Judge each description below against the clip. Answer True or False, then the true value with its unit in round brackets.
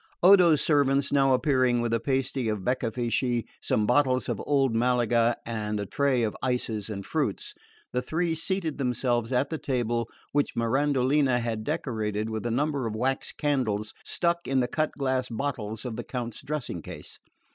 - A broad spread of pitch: False (3.4 semitones)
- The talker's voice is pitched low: True (125 Hz)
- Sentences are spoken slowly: False (170 wpm)